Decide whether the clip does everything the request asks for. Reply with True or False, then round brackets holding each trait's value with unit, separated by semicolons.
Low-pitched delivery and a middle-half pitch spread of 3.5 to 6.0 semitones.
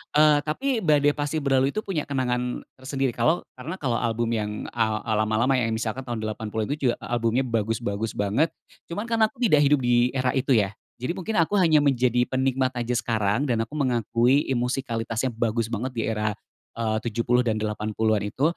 True (125 Hz; 3.8 semitones)